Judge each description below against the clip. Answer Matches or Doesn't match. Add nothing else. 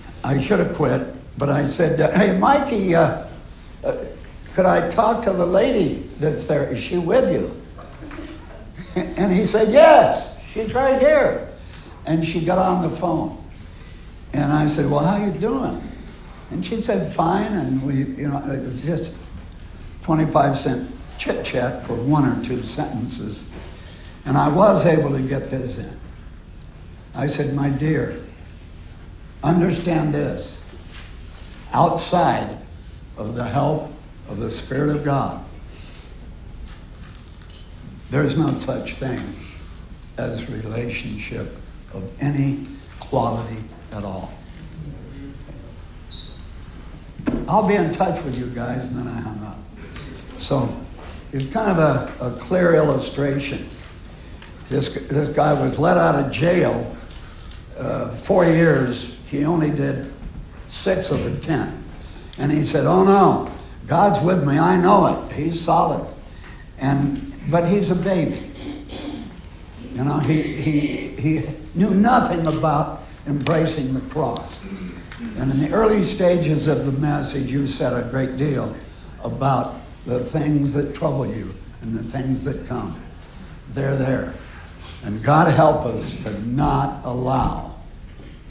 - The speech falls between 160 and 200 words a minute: Doesn't match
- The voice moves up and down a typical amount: Doesn't match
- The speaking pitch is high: Doesn't match